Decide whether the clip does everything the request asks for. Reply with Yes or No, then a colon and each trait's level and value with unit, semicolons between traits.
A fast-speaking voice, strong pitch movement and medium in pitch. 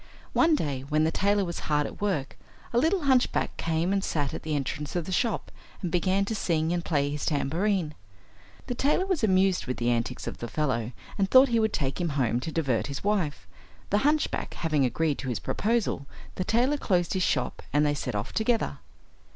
Yes: fast, 210 wpm; wide, 6.5 semitones; medium, 170 Hz